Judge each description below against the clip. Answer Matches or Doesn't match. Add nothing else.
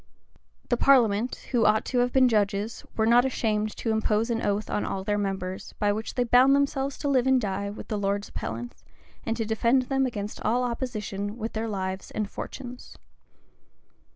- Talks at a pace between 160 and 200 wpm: Matches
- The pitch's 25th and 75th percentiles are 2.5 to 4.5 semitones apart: Matches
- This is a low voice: Doesn't match